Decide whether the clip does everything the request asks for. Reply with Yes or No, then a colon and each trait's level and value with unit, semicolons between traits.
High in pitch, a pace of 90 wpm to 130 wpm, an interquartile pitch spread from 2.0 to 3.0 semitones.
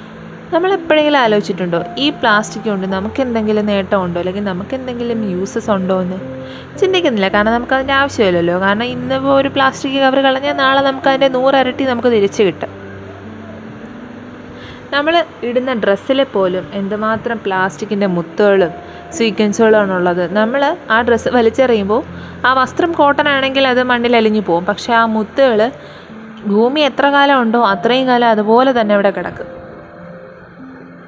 No: high, 230 Hz; fast, 125 wpm; average, 5.1 semitones